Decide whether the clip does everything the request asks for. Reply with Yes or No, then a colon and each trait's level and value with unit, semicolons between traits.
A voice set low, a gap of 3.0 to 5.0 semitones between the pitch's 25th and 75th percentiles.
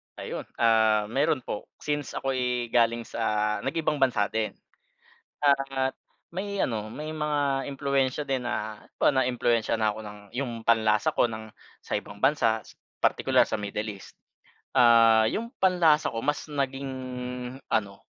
Yes: low, 125 Hz; average, 4.0 semitones